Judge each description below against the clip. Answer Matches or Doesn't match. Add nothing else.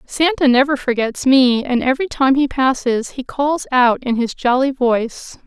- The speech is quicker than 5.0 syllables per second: Doesn't match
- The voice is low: Doesn't match